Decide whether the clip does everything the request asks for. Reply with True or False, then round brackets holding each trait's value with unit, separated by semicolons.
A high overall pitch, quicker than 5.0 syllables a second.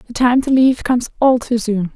True (240 Hz; 5.9 syllables/s)